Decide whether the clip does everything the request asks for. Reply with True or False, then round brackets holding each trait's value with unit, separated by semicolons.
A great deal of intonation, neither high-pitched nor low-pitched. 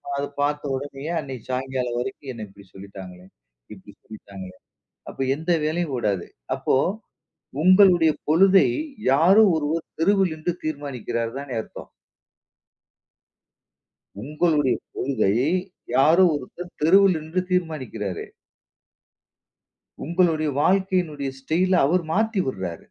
True (5.9 semitones; 150 Hz)